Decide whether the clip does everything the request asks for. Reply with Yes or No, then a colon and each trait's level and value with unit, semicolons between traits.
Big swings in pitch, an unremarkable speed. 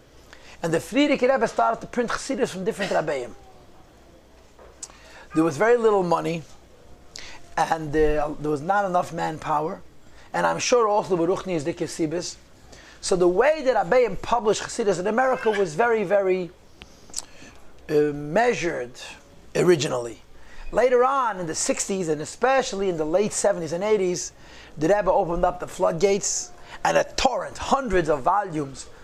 Yes: wide, 5.7 semitones; average, 145 wpm